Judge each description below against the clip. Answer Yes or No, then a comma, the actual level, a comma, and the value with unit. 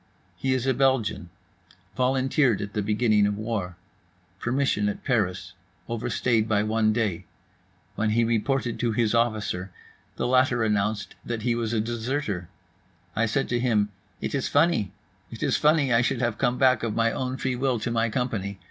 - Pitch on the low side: Yes, low, 115 Hz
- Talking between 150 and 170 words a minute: Yes, average, 165 wpm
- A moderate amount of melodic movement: Yes, average, 3.2 semitones